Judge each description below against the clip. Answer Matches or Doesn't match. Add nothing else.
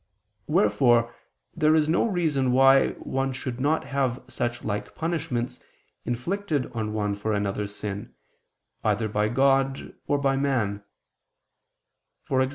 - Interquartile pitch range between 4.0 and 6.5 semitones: Matches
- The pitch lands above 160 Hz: Doesn't match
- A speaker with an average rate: Doesn't match